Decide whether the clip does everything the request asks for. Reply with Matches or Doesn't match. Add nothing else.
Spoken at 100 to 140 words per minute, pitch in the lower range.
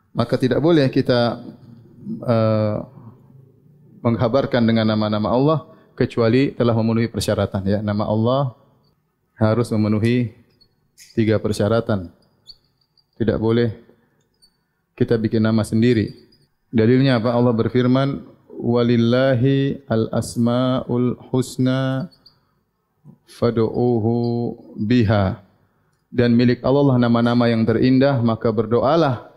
Doesn't match